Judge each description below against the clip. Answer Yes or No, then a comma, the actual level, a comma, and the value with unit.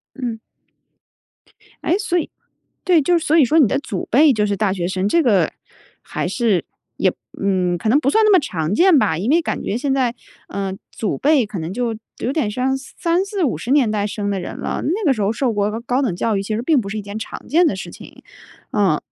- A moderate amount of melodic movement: No, wide, 6.7 semitones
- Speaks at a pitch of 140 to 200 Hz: No, high, 230 Hz